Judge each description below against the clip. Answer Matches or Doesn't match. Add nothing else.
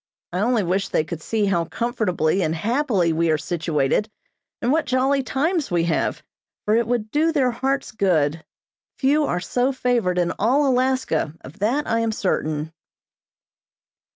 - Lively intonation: Matches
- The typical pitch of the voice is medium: Doesn't match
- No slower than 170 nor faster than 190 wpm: Doesn't match